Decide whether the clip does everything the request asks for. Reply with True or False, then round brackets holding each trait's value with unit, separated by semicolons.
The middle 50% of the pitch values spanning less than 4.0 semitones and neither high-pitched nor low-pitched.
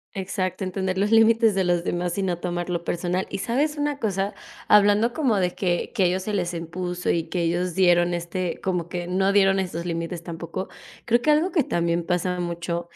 True (2.5 semitones; 180 Hz)